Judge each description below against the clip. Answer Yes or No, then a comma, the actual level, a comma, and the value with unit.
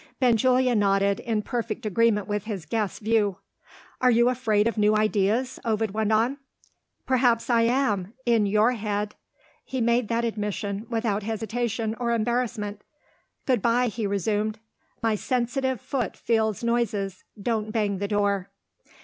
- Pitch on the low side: No, high, 220 Hz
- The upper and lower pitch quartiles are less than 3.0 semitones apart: Yes, narrow, 2.4 semitones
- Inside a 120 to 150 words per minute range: Yes, average, 140 wpm